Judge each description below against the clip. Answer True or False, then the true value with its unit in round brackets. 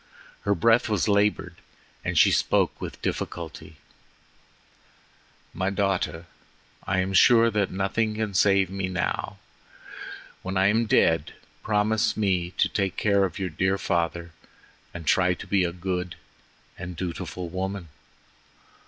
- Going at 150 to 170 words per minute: False (135 wpm)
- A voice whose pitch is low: True (95 Hz)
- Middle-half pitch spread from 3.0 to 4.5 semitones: False (2.4 semitones)